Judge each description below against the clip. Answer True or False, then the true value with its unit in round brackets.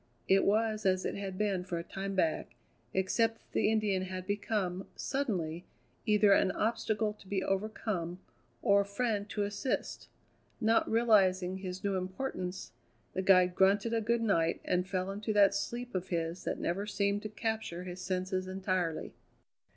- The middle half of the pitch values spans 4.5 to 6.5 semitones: False (2.6 semitones)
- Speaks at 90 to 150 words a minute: False (165 wpm)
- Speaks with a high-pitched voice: True (195 Hz)